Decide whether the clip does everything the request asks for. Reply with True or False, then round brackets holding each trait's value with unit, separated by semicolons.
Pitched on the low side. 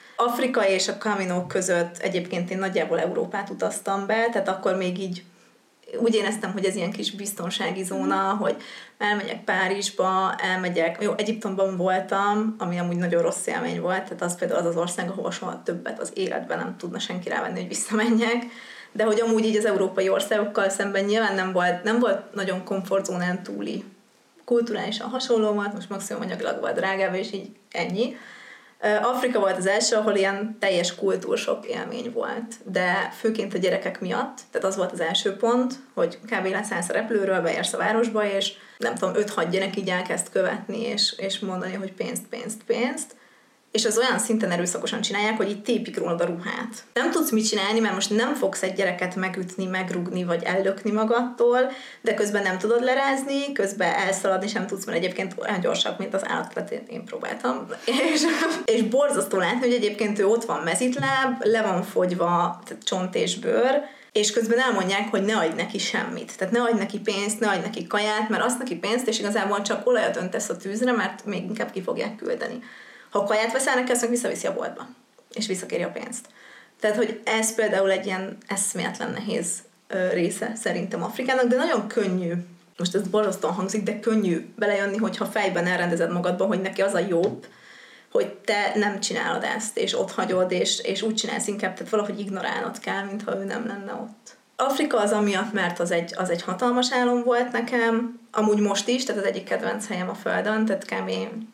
False (210 Hz)